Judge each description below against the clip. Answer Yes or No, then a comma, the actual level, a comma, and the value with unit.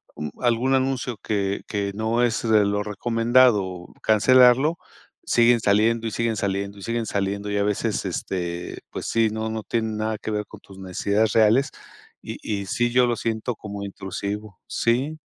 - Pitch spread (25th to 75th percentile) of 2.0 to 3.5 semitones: Yes, average, 2.7 semitones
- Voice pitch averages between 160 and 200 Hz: No, low, 110 Hz